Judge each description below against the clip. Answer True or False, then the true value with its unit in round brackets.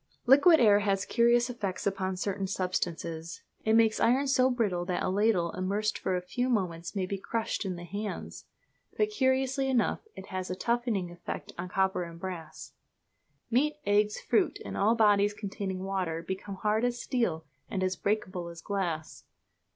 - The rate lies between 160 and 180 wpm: True (170 wpm)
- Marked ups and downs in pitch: False (4.2 semitones)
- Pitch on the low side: False (200 Hz)